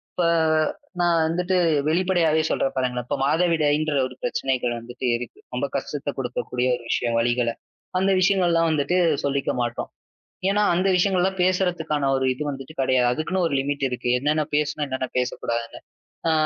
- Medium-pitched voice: Yes, medium, 145 Hz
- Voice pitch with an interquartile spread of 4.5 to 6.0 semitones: Yes, wide, 5.5 semitones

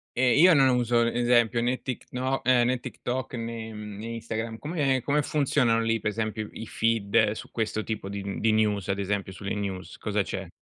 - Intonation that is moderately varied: Yes, average, 3.0 semitones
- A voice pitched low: Yes, low, 115 Hz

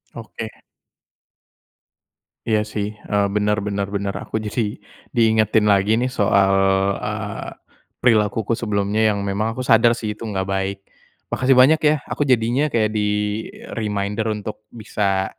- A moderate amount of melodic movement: No, narrow, 1.9 semitones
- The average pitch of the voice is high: No, low, 105 Hz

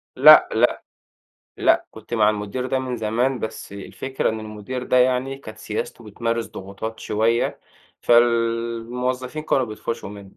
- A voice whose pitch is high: No, low, 115 Hz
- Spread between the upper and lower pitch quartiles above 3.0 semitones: No, average, 2.7 semitones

